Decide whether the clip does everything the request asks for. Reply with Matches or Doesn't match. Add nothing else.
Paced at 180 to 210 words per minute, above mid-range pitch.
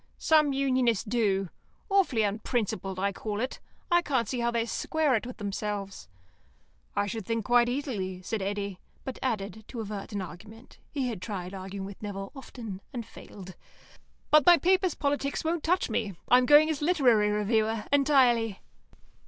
Doesn't match